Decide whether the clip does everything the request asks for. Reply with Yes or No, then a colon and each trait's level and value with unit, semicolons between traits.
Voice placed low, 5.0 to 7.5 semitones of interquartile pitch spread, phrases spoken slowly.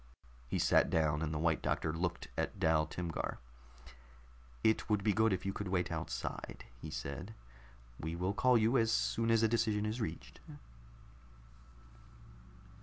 No: very low, 95 Hz; wide, 5.5 semitones; average, 155 wpm